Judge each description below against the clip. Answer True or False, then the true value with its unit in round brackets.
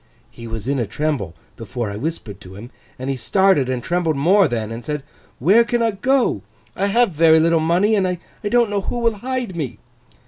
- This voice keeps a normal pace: False (210 wpm)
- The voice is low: False (160 Hz)